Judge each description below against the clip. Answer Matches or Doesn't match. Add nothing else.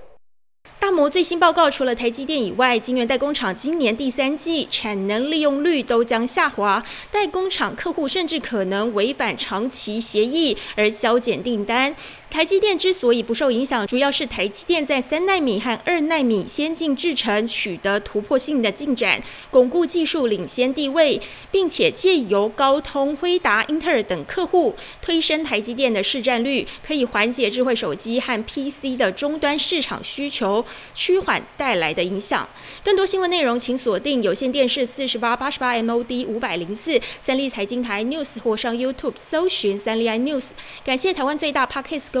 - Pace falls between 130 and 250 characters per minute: Doesn't match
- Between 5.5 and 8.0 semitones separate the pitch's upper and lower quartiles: Doesn't match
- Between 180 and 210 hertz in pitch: Doesn't match